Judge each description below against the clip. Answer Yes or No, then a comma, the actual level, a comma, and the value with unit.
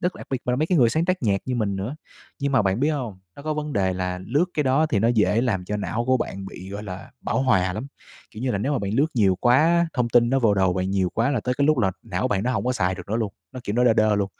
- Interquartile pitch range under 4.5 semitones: No, average, 5.2 semitones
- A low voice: Yes, low, 115 Hz